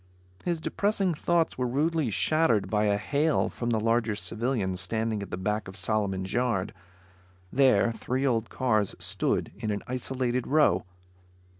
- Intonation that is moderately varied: Yes, average, 4.4 semitones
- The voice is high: No, low, 115 Hz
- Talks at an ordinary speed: Yes, average, 150 wpm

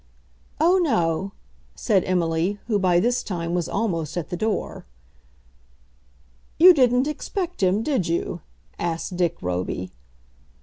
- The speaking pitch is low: No, medium, 185 Hz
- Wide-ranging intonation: Yes, wide, 6.5 semitones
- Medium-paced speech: No, slow, 125 wpm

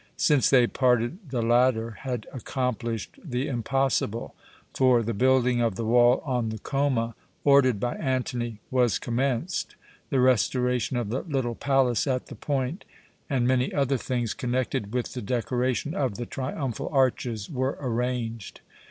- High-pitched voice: No, low, 125 Hz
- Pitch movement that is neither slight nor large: No, narrow, 2.0 semitones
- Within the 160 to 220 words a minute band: No, average, 145 wpm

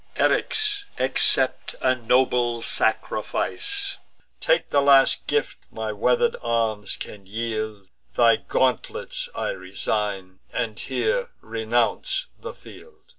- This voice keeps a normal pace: No, slow, 105 wpm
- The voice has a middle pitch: No, low, 120 Hz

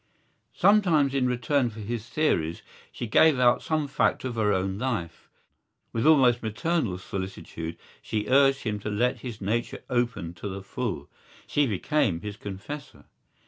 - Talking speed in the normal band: Yes, average, 150 wpm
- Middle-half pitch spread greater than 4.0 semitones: Yes, average, 5.2 semitones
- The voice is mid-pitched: No, low, 115 Hz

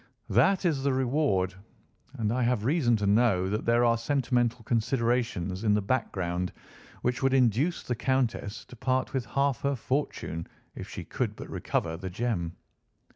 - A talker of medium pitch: No, low, 120 Hz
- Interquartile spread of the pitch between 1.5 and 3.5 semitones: No, average, 4.1 semitones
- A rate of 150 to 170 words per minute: Yes, average, 165 wpm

